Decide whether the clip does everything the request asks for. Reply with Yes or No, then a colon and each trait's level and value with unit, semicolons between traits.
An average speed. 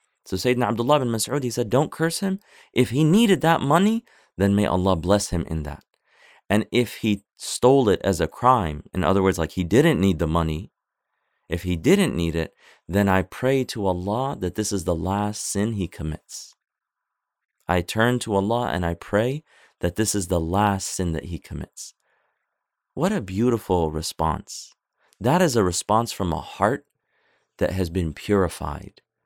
Yes: average, 180 wpm